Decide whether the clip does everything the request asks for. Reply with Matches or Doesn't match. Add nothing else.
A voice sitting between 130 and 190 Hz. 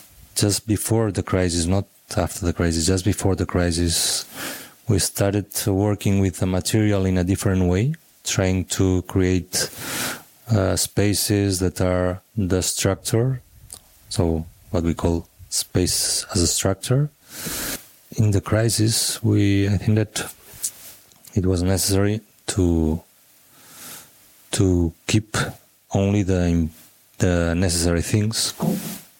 Doesn't match